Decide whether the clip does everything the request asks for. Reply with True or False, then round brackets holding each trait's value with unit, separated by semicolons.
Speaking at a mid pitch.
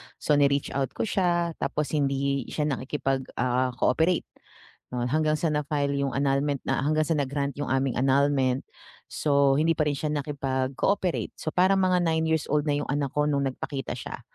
True (145 Hz)